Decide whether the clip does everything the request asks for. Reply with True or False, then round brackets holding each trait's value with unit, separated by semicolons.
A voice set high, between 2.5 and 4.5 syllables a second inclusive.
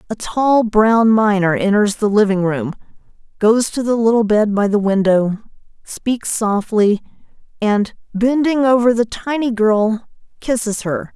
True (220 Hz; 4.1 syllables/s)